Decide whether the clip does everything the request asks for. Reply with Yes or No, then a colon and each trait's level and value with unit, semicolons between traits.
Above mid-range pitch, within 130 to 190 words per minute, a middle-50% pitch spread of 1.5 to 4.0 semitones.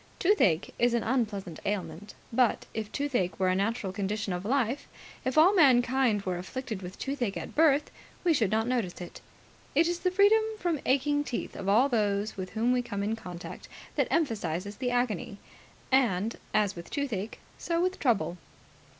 No: high, 225 Hz; average, 175 wpm; wide, 5.4 semitones